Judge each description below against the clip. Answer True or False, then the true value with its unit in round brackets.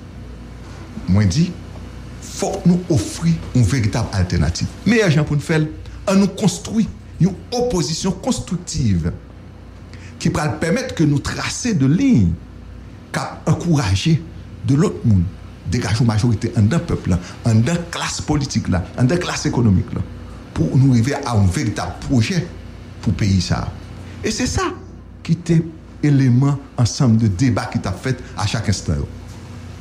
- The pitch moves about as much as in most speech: False (7.5 semitones)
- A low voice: True (115 Hz)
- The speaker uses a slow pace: False (145 wpm)